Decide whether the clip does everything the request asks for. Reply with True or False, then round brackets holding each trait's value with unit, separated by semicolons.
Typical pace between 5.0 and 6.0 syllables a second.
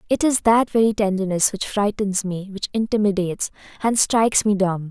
True (5.3 syllables/s)